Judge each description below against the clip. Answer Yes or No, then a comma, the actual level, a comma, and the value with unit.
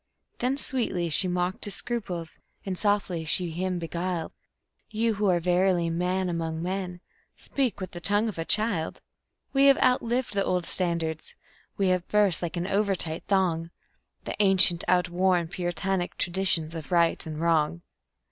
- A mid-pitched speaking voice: Yes, medium, 180 Hz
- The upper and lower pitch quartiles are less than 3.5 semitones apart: Yes, average, 2.8 semitones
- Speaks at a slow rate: No, average, 155 wpm